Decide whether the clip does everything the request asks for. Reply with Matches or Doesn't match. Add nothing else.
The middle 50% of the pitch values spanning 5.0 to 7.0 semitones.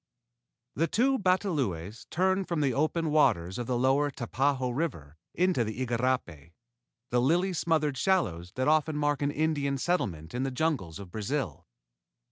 Matches